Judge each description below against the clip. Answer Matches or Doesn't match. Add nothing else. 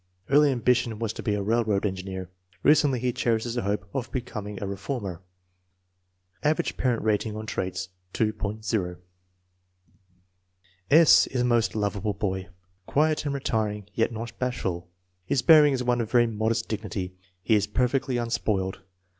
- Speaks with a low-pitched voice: Matches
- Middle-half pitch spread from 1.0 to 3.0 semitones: Doesn't match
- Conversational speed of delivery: Matches